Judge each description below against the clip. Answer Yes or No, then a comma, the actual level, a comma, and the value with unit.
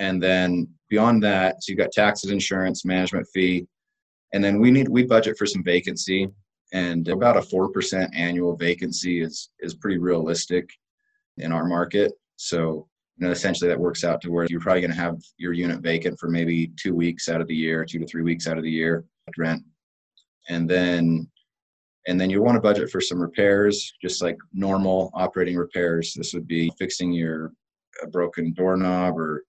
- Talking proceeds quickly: No, average, 190 wpm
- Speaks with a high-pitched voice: No, very low, 90 Hz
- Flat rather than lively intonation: Yes, narrow, 2.0 semitones